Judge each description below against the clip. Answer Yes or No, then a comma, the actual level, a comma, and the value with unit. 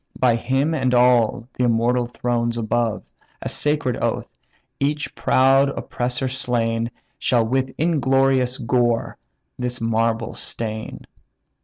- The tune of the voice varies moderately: No, narrow, 2.2 semitones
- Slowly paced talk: Yes, slow, 115 wpm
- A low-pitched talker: Yes, low, 125 Hz